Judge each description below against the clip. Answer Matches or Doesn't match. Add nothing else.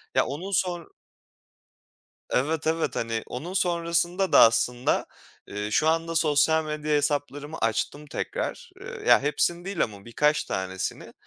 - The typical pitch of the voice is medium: Matches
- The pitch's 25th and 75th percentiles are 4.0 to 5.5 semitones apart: Matches